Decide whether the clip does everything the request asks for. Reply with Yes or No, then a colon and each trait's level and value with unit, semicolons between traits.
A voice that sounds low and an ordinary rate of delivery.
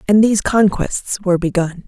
No: high, 190 Hz; average, 160 wpm